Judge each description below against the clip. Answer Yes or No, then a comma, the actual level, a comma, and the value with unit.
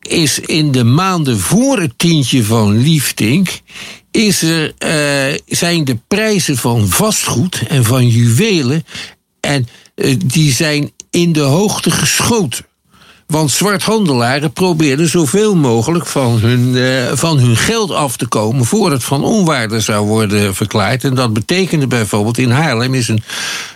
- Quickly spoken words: No, average, 140 wpm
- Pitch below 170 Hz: Yes, medium, 140 Hz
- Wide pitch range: Yes, wide, 5.9 semitones